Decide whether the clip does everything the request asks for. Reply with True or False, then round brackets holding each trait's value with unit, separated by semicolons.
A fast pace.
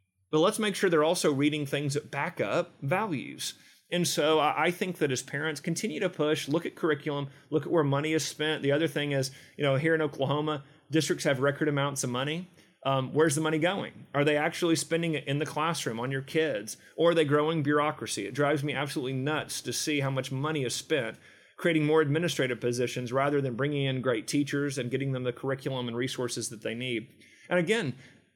True (215 wpm)